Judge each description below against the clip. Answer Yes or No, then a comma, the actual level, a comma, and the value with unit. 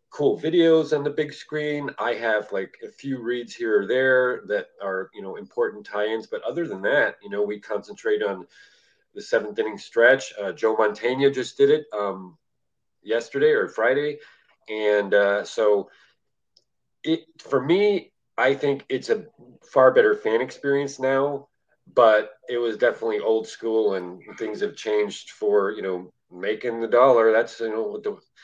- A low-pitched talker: No, medium, 160 Hz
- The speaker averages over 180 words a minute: No, average, 170 wpm